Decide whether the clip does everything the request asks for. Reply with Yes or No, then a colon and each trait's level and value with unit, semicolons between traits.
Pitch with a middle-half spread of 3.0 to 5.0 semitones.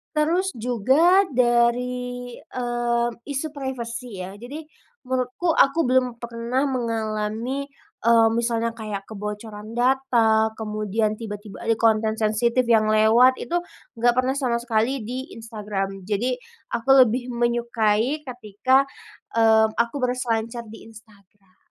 No: narrow, 2.5 semitones